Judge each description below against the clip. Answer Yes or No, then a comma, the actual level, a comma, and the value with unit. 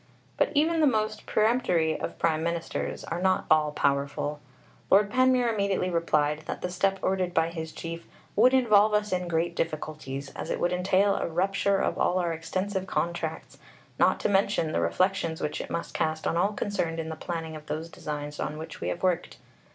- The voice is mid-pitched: Yes, medium, 170 Hz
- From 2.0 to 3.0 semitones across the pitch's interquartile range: No, average, 3.8 semitones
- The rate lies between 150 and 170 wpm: No, average, 190 wpm